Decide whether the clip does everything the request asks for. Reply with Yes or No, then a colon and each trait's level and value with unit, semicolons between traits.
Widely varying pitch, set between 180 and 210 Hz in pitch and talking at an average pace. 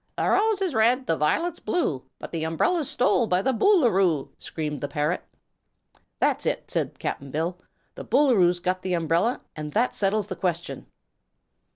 Yes: wide, 7.5 semitones; medium, 185 Hz; average, 175 wpm